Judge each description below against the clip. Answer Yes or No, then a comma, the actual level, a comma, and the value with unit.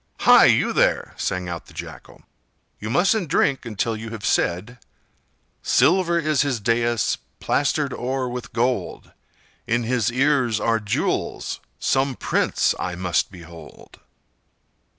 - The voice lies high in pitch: No, low, 120 Hz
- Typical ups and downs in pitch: Yes, average, 4.7 semitones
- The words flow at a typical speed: No, slow, 125 wpm